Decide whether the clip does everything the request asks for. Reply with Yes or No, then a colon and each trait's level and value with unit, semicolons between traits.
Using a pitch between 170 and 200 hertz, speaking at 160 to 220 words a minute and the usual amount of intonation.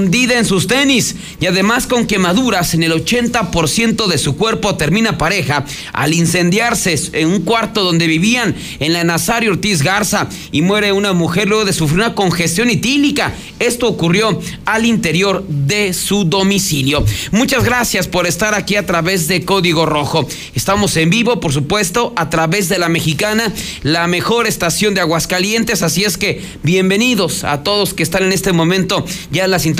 Yes: high, 190 Hz; average, 165 wpm; average, 4.2 semitones